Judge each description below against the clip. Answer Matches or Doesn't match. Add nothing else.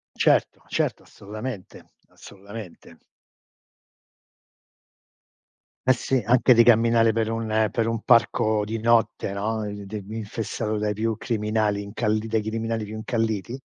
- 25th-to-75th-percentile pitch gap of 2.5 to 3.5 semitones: Doesn't match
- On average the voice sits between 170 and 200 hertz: Doesn't match